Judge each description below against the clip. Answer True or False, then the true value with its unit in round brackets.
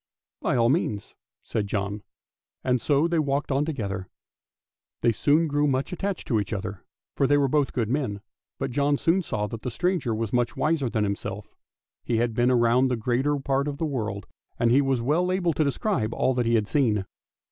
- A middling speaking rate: False (210 wpm)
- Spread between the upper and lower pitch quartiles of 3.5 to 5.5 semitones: True (4.7 semitones)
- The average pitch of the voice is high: False (130 Hz)